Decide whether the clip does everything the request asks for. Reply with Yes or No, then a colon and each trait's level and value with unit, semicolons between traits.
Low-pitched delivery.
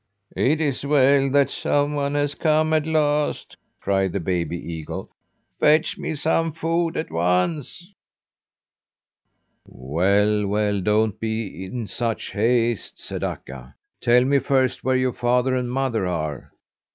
Yes: low, 125 Hz